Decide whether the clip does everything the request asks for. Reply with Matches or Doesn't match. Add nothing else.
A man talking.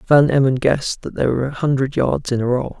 Matches